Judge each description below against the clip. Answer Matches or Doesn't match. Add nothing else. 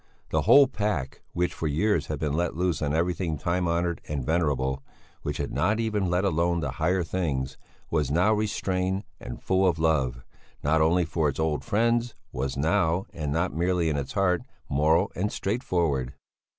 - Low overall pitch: Matches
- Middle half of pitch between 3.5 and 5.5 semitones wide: Matches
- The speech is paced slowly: Doesn't match